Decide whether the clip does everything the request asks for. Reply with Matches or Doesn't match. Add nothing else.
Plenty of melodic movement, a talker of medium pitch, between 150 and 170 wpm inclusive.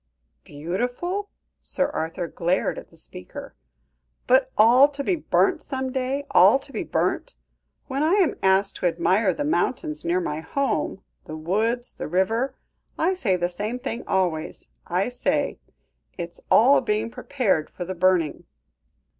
Doesn't match